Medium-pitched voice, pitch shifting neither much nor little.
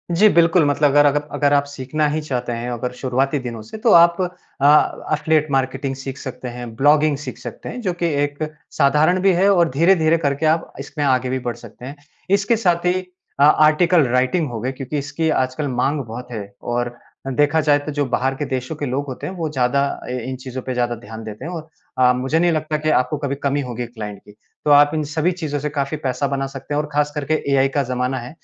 Yes: medium, 145 Hz; average, 3.3 semitones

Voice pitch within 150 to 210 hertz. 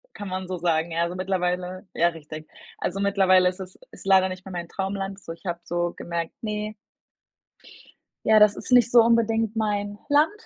Yes: high, 190 Hz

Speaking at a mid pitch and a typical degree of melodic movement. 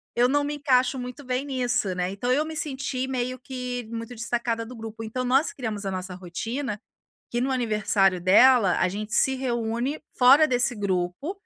No: high, 245 Hz; average, 3.6 semitones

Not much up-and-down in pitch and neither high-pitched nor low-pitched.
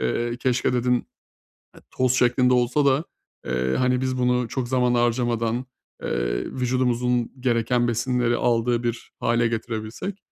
No: narrow, 1.3 semitones; low, 120 Hz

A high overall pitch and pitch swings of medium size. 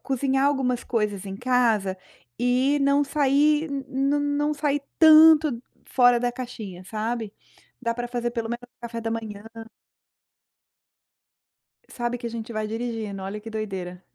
Yes: high, 240 Hz; average, 3.9 semitones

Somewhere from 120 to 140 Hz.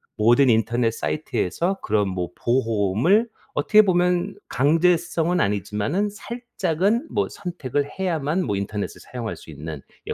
Yes: low, 135 Hz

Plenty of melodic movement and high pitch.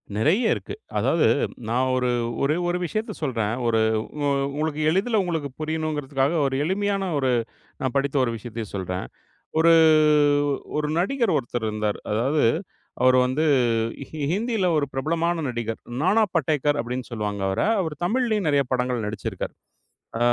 No: wide, 6.1 semitones; medium, 145 Hz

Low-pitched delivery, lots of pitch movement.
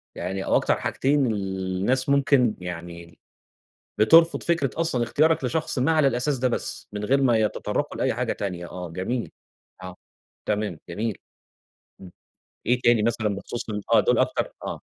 Yes: low, 110 Hz; wide, 5.8 semitones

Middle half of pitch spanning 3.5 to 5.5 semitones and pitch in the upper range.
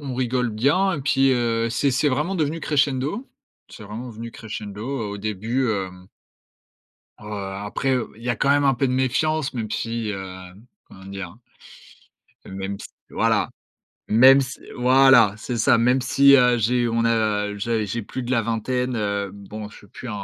No: average, 3.9 semitones; low, 115 Hz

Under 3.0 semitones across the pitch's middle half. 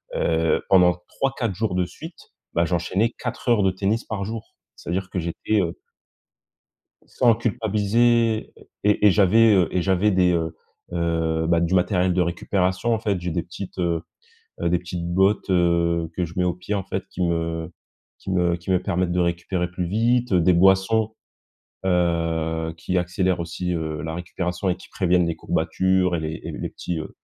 Yes: narrow, 2.5 semitones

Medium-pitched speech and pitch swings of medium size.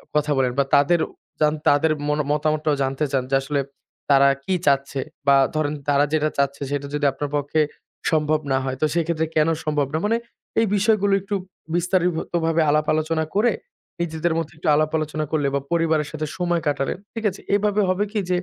Yes: medium, 155 Hz; average, 3.0 semitones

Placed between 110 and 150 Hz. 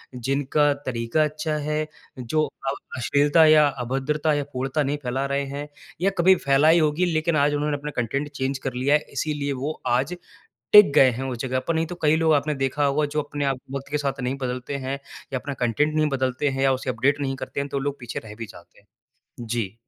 Yes: medium, 140 Hz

